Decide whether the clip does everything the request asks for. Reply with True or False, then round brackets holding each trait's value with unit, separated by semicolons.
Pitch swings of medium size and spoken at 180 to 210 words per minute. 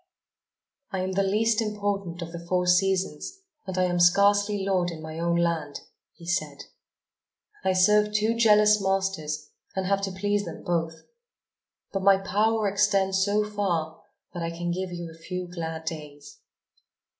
False (3.0 semitones; 155 wpm)